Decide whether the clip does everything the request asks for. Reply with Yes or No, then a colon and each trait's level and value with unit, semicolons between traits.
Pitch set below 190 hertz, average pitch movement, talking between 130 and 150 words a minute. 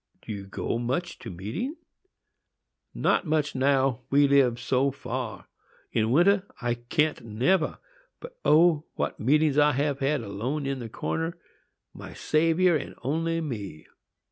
Yes: medium, 140 Hz; average, 4.8 semitones; average, 140 wpm